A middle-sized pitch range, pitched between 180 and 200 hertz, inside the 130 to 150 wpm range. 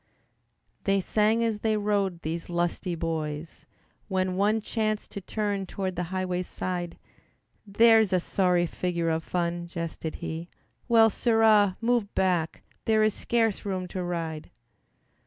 Yes: average, 3.7 semitones; medium, 185 Hz; average, 140 wpm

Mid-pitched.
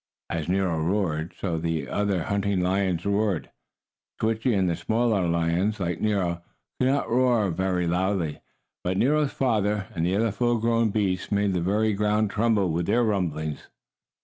No: low, 100 Hz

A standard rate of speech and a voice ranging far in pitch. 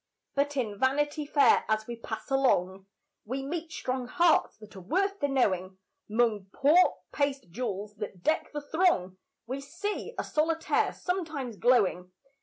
Yes: average, 150 wpm; wide, 6.6 semitones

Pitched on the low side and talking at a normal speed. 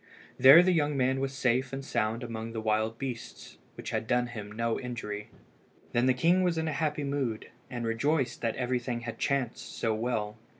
Yes: low, 125 Hz; average, 195 wpm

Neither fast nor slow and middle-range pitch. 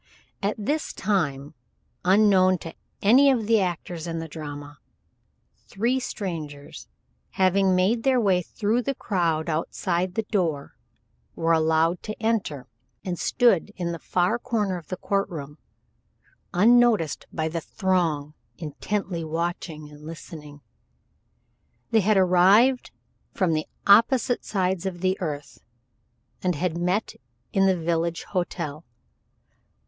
No: slow, 130 wpm; medium, 180 Hz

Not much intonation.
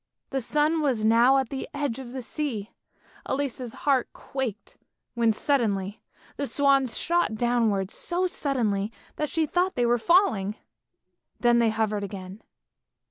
No: average, 4.5 semitones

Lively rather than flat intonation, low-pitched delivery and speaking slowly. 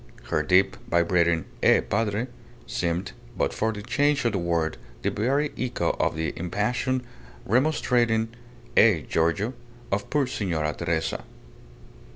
Yes: wide, 6.1 semitones; low, 105 Hz; slow, 130 wpm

